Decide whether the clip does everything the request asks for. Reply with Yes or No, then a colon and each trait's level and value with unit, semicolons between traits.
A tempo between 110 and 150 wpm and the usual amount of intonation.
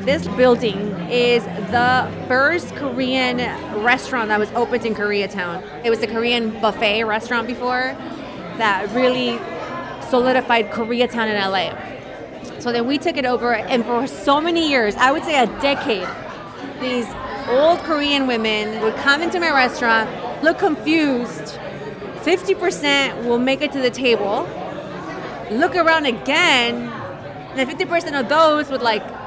Yes: average, 140 wpm; average, 3.6 semitones